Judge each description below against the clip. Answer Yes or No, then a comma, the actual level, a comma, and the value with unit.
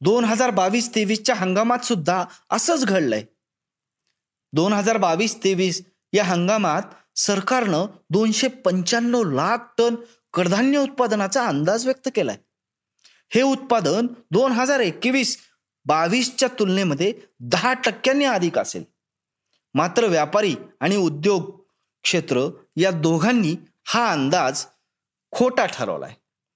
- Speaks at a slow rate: No, average, 105 wpm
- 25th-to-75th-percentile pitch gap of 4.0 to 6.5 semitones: Yes, average, 4.8 semitones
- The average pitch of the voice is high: Yes, high, 215 Hz